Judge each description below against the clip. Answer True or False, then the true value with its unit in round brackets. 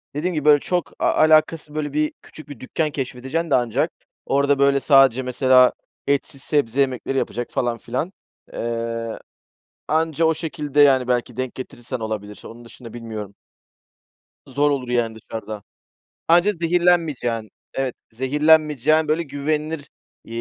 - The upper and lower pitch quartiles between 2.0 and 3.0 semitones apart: False (4.2 semitones)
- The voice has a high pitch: False (140 Hz)